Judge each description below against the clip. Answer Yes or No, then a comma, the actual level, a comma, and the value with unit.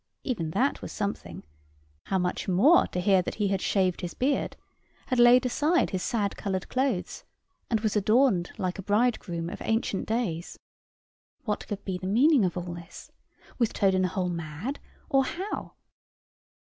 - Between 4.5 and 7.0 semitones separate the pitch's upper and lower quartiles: Yes, average, 5.1 semitones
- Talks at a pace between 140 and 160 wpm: No, average, 170 wpm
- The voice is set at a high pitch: Yes, high, 200 Hz